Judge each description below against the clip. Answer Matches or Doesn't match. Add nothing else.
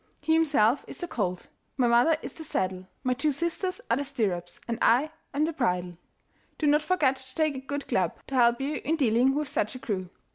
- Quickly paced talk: Matches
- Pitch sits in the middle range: Doesn't match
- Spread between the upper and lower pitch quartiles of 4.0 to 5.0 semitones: Matches